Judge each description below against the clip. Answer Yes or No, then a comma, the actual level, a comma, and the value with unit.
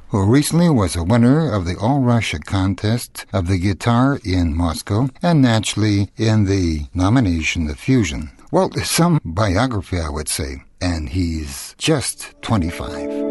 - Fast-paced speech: No, average, 145 wpm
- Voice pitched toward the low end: Yes, low, 100 Hz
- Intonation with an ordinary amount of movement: No, wide, 6.1 semitones